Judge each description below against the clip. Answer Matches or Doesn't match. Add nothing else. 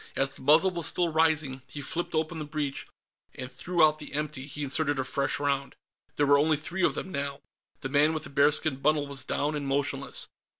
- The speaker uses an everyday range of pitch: Doesn't match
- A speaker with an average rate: Doesn't match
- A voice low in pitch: Doesn't match